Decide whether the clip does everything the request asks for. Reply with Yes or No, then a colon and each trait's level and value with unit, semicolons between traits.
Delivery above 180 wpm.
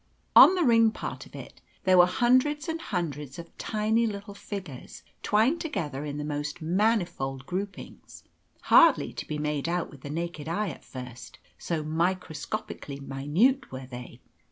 No: average, 155 wpm